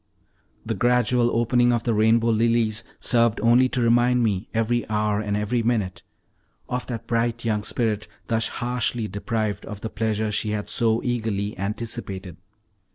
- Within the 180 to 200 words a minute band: No, average, 155 wpm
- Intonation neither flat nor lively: No, narrow, 2.0 semitones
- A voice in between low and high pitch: No, low, 115 Hz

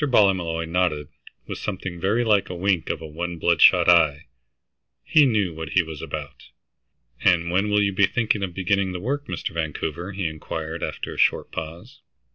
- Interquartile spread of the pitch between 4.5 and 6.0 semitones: No, average, 3.5 semitones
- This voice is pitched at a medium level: No, very low, 90 Hz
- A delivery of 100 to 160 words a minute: No, average, 175 wpm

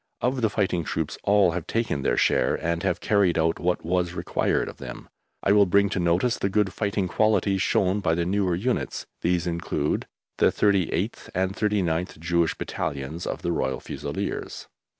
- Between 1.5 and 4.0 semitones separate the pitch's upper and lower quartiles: Yes, average, 3.1 semitones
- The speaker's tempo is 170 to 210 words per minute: Yes, average, 175 wpm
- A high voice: No, very low, 90 Hz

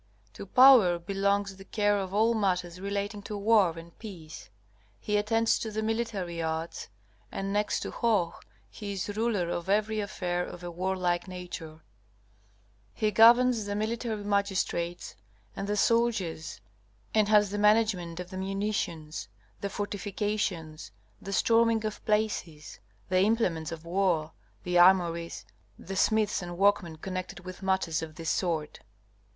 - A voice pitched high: Yes, high, 195 Hz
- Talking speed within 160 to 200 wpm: No, average, 145 wpm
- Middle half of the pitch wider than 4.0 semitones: No, average, 3.4 semitones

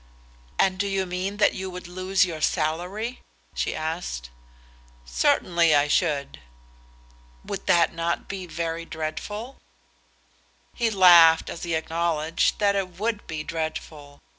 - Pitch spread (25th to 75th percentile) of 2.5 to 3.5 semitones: Yes, average, 3.2 semitones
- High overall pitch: No, medium, 170 Hz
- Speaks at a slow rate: Yes, slow, 130 wpm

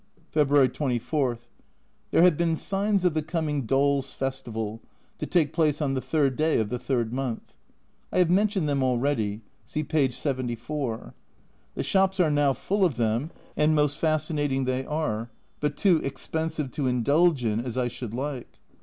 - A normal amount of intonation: Yes, average, 3.9 semitones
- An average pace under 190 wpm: Yes, average, 165 wpm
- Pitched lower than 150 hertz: Yes, medium, 140 Hz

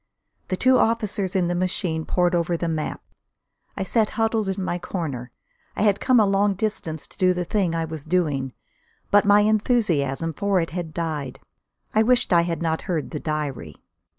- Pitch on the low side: No, medium, 180 Hz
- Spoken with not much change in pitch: No, average, 4.2 semitones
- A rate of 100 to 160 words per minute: No, average, 185 wpm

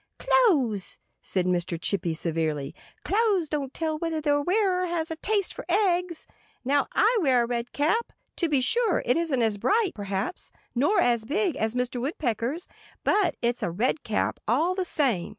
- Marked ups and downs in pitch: Yes, wide, 7.7 semitones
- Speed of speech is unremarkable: Yes, average, 170 wpm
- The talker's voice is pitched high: Yes, very high, 290 Hz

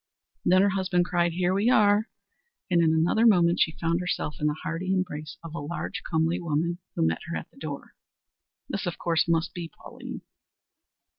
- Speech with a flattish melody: Yes, narrow, 2.2 semitones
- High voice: No, medium, 170 Hz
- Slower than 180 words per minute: No, average, 190 wpm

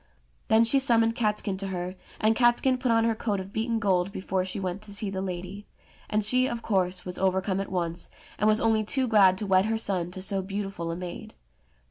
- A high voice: Yes, high, 200 Hz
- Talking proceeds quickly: Yes, fast, 220 wpm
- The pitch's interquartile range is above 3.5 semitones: No, average, 3.1 semitones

